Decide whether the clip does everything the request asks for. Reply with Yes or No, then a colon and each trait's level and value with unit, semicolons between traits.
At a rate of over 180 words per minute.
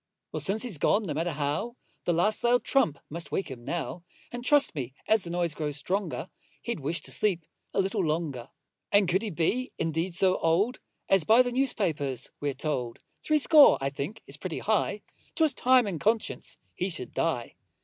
Yes: average, 190 wpm